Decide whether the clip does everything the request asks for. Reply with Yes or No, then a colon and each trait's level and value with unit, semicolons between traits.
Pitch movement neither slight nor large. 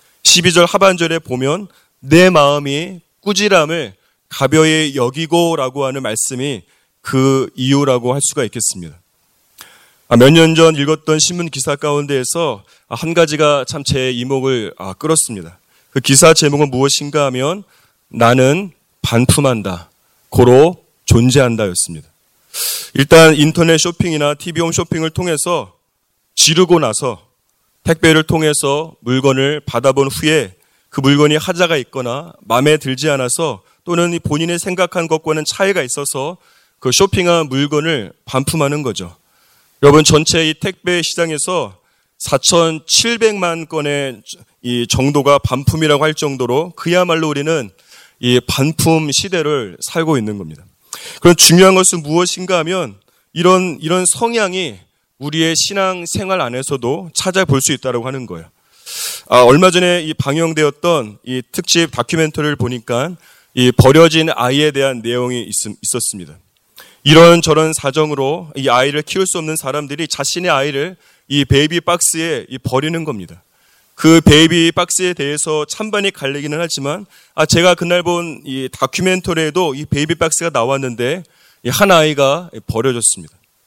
Yes: average, 4.1 semitones